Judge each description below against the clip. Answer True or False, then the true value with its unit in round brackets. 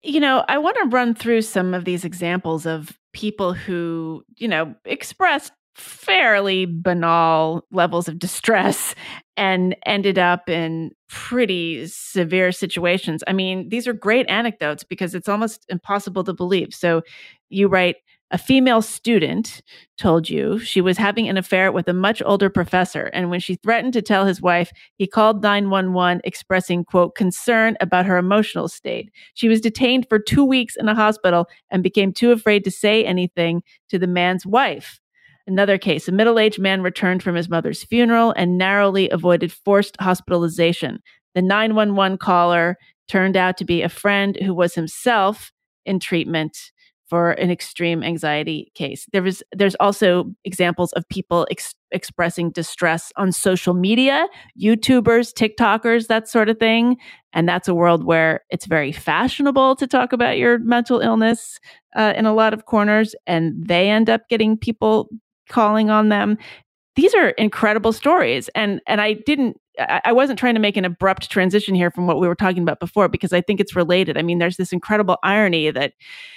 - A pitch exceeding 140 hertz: True (190 Hz)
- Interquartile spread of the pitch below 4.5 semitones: True (3.9 semitones)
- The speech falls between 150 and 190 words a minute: True (170 wpm)